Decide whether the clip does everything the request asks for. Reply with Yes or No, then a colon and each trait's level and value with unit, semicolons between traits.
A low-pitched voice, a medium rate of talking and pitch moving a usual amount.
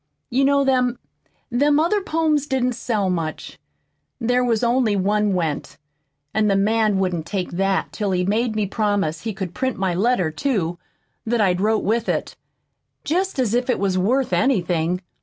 No: high, 215 Hz; average, 170 wpm; average, 5.0 semitones